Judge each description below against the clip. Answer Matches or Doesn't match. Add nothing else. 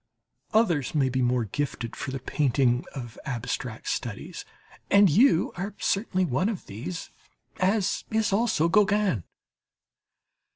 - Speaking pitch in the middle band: Matches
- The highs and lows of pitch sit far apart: Matches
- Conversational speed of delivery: Doesn't match